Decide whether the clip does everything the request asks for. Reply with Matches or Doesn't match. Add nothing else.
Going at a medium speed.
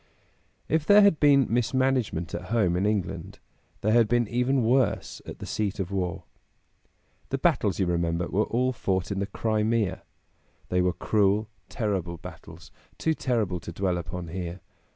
Matches